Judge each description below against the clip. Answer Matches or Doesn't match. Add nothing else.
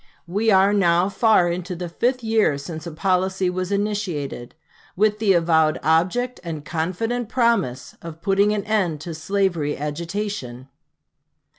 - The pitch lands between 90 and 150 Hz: Doesn't match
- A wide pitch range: Doesn't match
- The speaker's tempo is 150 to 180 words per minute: Doesn't match